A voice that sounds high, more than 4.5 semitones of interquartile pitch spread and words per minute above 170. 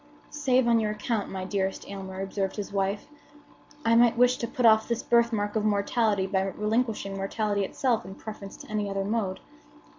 No: high, 210 Hz; average, 2.9 semitones; average, 180 wpm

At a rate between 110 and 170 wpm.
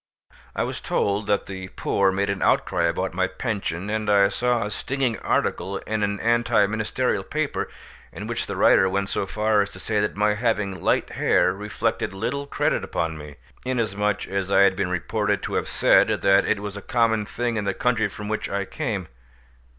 No: average, 195 wpm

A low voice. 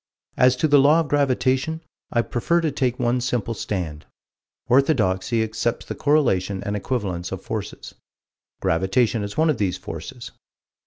Yes: low, 120 Hz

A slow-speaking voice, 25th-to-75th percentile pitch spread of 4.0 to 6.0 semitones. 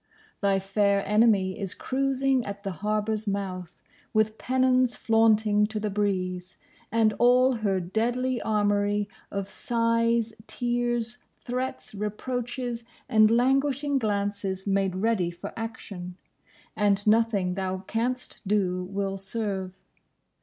No: slow, 115 wpm; average, 3.3 semitones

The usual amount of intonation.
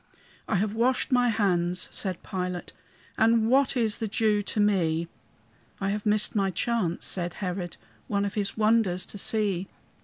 Yes: average, 3.4 semitones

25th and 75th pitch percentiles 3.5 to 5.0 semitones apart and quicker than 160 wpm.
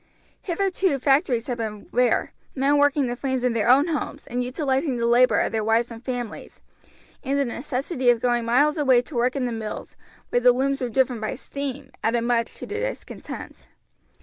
No: average, 2.8 semitones; average, 195 wpm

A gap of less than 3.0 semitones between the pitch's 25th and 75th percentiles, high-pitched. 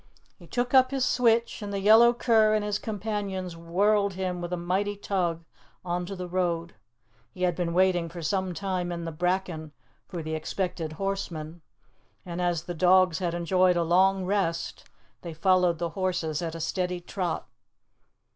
No: narrow, 2.6 semitones; medium, 180 Hz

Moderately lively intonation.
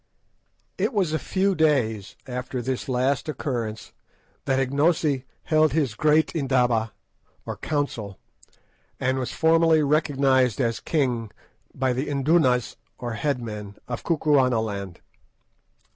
Yes: average, 4.1 semitones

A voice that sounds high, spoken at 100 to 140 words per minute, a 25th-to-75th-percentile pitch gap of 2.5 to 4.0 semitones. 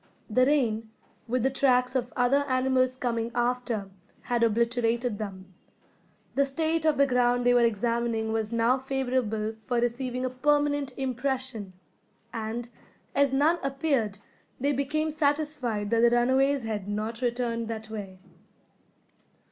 Yes: high, 245 Hz; slow, 135 wpm; average, 2.9 semitones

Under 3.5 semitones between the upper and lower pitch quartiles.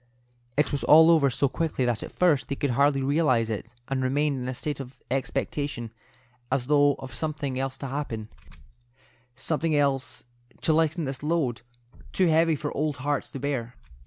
Yes: average, 2.7 semitones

